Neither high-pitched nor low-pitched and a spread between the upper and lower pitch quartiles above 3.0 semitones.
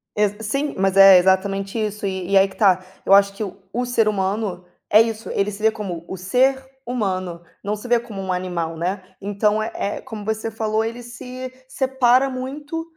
No: high, 210 Hz; average, 3.7 semitones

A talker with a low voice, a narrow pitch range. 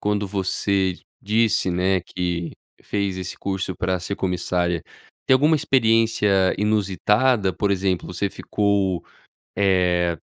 Yes: very low, 95 Hz; narrow, 2.2 semitones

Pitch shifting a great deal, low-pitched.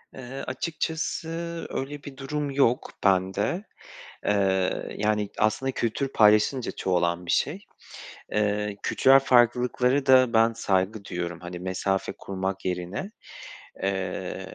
Yes: wide, 5.8 semitones; low, 105 Hz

